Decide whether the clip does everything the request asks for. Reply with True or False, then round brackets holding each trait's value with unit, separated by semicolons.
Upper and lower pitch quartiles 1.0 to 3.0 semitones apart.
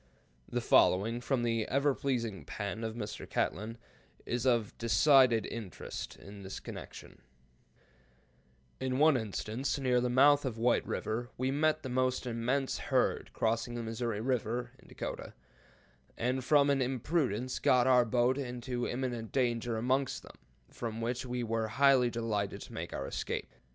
True (2.4 semitones)